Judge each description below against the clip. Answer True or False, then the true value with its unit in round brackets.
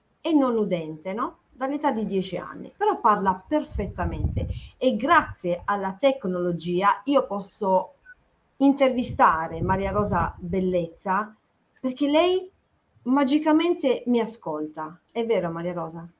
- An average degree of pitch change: False (7.5 semitones)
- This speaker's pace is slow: True (110 wpm)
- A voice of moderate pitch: False (210 Hz)